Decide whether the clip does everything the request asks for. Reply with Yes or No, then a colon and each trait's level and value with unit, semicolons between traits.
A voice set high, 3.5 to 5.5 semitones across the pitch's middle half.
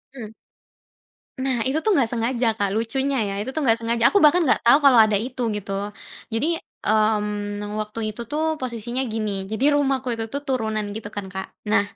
Yes: high, 230 Hz; average, 3.8 semitones